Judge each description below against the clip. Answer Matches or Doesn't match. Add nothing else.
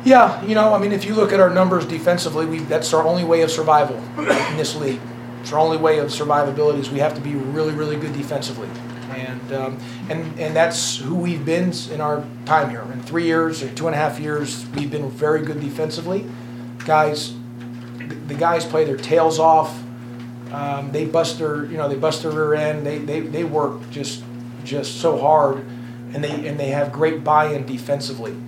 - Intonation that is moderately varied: Matches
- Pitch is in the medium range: Matches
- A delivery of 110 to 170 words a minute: Doesn't match